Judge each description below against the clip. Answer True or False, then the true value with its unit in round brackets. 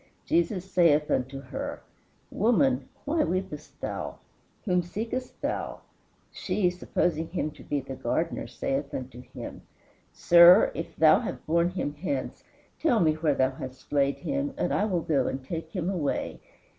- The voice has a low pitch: False (165 Hz)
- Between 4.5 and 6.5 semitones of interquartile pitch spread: True (5.1 semitones)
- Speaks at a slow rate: False (155 wpm)